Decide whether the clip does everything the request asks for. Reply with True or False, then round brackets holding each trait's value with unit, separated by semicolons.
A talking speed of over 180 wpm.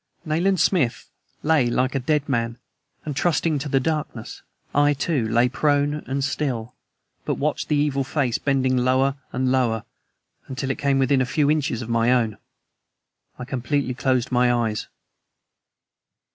False (155 wpm)